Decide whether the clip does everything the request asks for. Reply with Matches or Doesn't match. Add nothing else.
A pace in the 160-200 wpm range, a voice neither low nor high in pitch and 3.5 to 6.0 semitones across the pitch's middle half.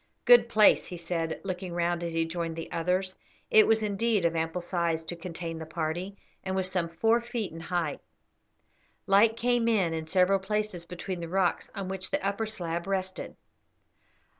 Doesn't match